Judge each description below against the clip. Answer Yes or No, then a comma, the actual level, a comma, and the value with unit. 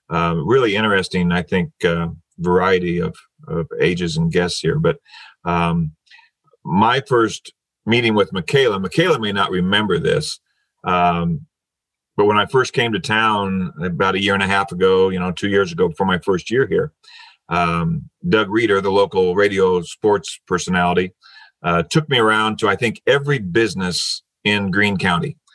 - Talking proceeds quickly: No, average, 165 wpm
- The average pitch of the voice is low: Yes, very low, 95 Hz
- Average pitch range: Yes, average, 3.1 semitones